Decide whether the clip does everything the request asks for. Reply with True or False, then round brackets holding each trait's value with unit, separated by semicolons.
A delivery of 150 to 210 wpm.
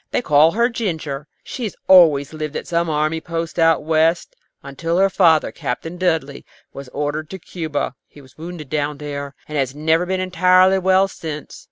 True (180 wpm)